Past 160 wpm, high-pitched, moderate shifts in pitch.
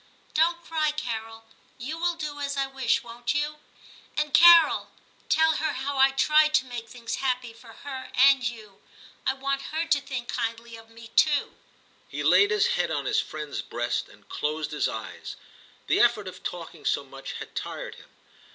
Yes: average, 180 wpm; very high, 265 Hz; average, 4.9 semitones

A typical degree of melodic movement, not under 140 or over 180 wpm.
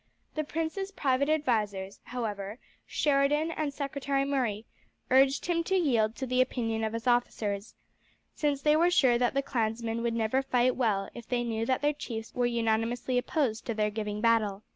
Yes: average, 3.9 semitones; average, 175 wpm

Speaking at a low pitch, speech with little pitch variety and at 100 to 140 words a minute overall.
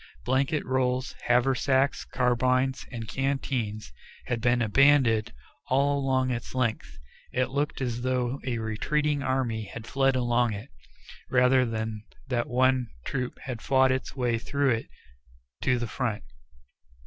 Yes: low, 125 Hz; narrow, 2.1 semitones; slow, 135 wpm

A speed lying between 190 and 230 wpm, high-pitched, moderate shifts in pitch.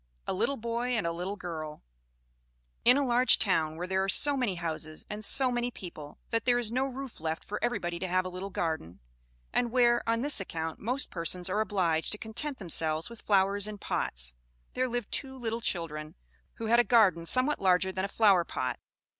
No: fast, 205 wpm; high, 200 Hz; wide, 6.0 semitones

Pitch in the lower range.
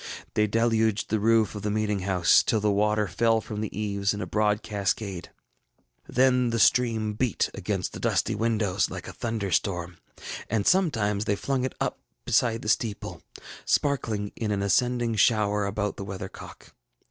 Yes: low, 105 Hz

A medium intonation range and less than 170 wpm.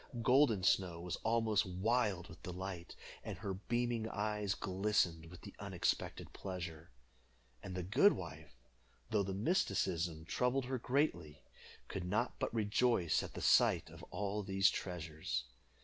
Yes: average, 4.4 semitones; average, 140 wpm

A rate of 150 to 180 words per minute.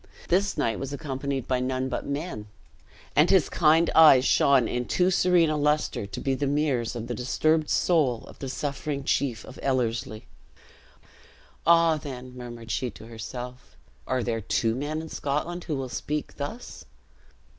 Yes: average, 165 wpm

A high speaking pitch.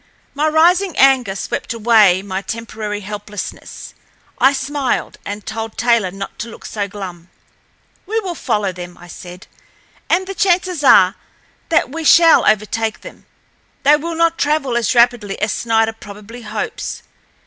Yes: high, 225 Hz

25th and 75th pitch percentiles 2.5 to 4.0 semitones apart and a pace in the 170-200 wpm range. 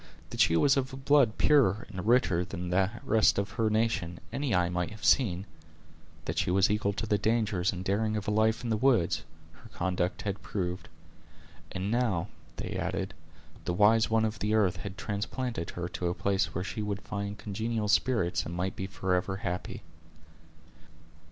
Yes: average, 3.3 semitones; average, 185 wpm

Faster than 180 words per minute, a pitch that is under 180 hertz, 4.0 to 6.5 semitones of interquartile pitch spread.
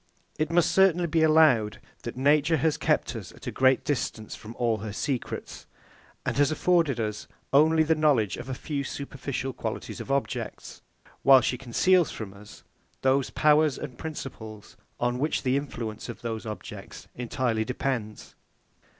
No: average, 160 wpm; low, 135 Hz; average, 5.0 semitones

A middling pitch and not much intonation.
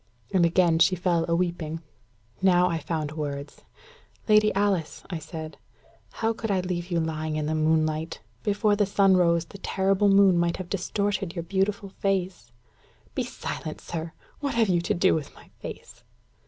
No: medium, 175 Hz; average, 3.4 semitones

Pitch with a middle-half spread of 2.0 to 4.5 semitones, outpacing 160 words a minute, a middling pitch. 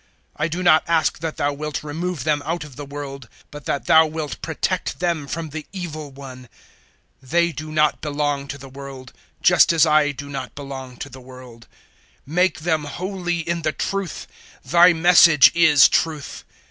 Yes: average, 3.1 semitones; average, 185 wpm; medium, 150 Hz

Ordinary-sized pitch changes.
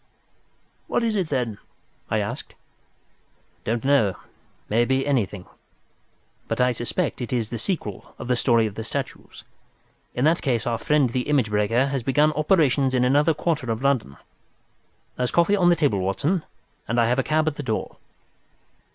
Yes: average, 4.6 semitones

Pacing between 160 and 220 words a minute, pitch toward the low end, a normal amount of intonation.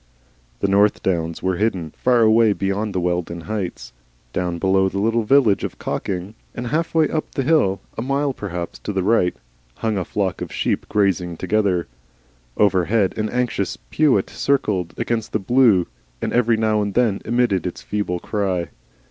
Yes: average, 175 wpm; low, 100 Hz; average, 3.8 semitones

